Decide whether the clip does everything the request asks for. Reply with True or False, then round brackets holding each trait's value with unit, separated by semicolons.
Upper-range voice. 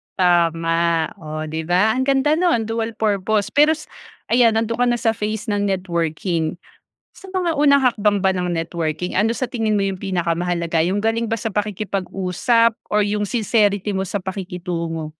True (200 Hz)